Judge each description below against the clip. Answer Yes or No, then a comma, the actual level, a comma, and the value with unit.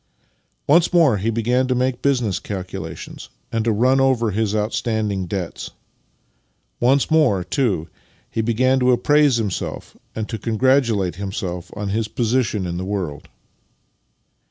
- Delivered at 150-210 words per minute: No, slow, 135 wpm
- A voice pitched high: No, low, 115 Hz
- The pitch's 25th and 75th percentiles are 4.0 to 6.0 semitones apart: Yes, average, 4.4 semitones